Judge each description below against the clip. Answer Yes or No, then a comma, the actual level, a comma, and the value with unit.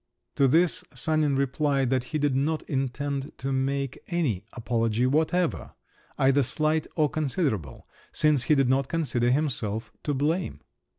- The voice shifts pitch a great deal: No, average, 3.0 semitones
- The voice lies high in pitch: No, medium, 140 Hz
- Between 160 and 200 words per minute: No, average, 140 wpm